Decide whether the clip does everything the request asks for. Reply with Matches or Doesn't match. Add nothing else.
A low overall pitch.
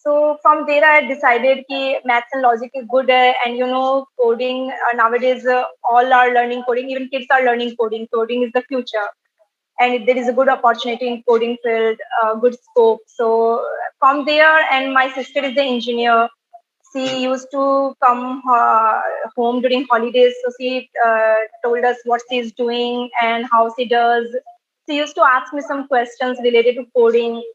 Doesn't match